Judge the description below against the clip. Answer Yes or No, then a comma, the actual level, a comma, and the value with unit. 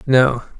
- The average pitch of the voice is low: Yes, low, 125 Hz